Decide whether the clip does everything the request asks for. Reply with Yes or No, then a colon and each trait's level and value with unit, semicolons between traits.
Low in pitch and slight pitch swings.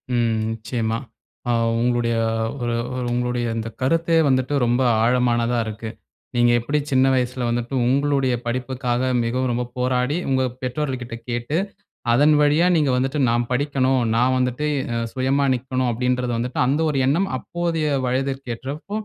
Yes: low, 125 Hz; narrow, 2.2 semitones